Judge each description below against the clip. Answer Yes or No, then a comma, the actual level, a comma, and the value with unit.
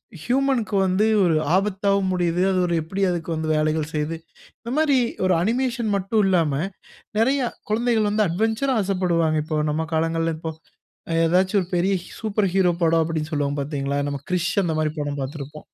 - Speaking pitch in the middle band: Yes, medium, 175 Hz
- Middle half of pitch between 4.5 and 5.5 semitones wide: Yes, average, 4.8 semitones